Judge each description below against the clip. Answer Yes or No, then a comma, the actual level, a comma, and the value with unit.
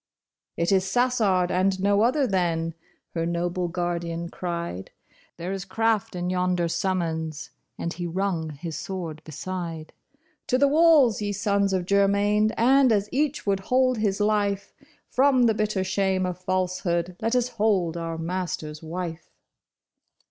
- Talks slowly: No, average, 155 wpm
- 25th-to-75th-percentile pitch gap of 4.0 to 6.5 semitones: No, average, 3.6 semitones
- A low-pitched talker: No, medium, 185 Hz